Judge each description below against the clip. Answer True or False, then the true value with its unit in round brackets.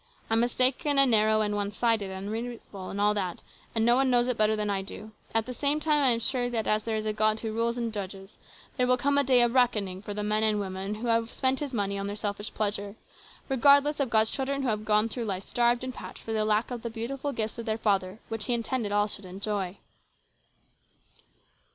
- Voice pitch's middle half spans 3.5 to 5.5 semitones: False (3.0 semitones)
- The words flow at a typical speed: False (235 wpm)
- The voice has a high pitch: True (220 Hz)